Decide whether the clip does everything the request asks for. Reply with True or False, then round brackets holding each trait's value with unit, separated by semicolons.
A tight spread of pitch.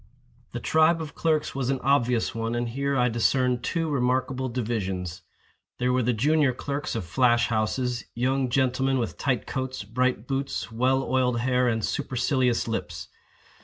True (2.2 semitones)